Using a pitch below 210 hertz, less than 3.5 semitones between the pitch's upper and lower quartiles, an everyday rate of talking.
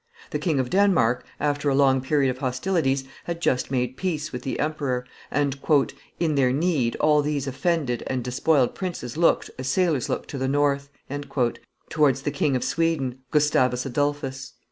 Yes: medium, 140 Hz; average, 2.9 semitones; average, 165 wpm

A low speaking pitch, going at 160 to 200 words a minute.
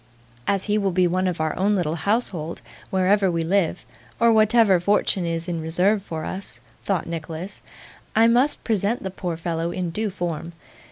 No: medium, 185 Hz; average, 175 wpm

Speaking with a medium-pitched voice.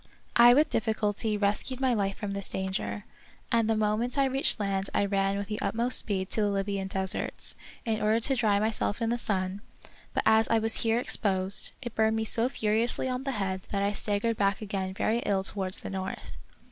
No: high, 210 Hz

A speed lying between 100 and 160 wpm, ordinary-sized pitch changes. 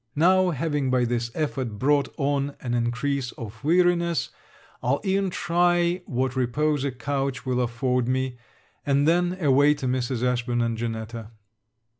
Yes: average, 145 wpm; average, 3.9 semitones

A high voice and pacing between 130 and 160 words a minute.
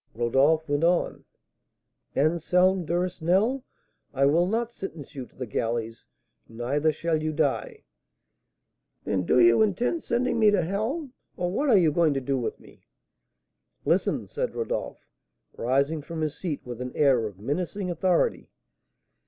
No: medium, 160 Hz; average, 150 wpm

